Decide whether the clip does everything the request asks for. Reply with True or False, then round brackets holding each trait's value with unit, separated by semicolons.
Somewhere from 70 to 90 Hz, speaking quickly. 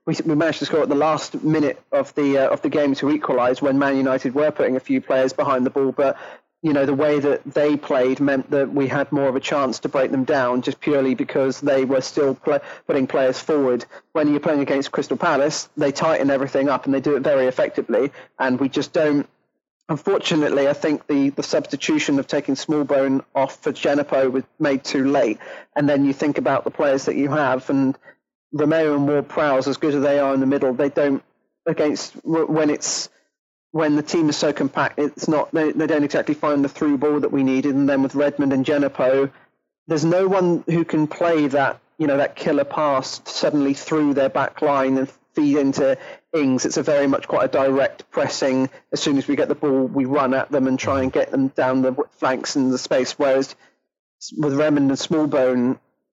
False (140 Hz; 215 wpm)